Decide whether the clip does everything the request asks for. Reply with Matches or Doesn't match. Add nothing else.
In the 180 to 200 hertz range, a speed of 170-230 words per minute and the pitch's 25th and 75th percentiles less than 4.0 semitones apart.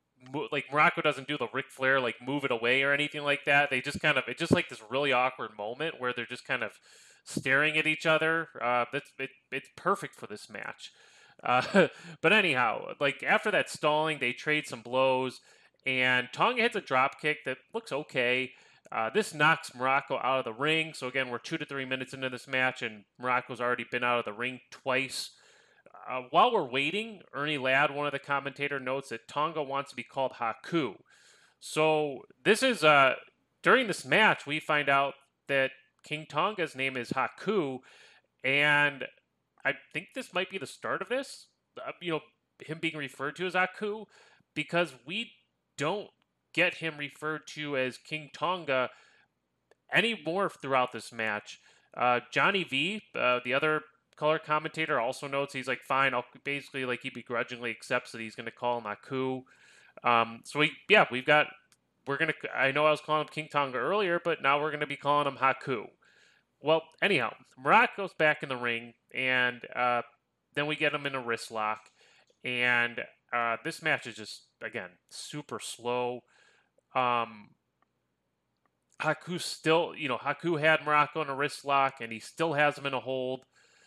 Doesn't match